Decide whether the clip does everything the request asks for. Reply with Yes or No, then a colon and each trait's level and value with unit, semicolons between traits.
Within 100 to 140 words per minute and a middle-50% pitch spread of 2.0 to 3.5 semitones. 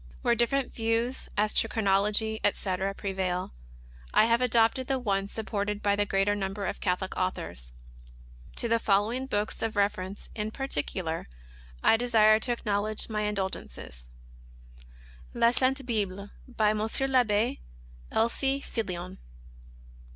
Yes: slow, 135 wpm; average, 2.9 semitones